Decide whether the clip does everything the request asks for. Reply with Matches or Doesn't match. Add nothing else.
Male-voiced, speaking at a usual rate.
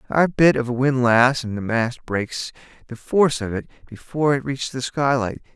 Matches